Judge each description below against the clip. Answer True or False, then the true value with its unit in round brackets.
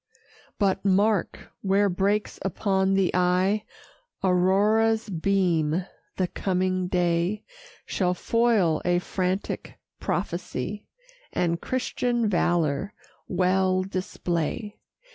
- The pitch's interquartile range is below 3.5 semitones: True (2.4 semitones)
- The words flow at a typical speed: False (85 wpm)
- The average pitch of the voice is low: False (185 Hz)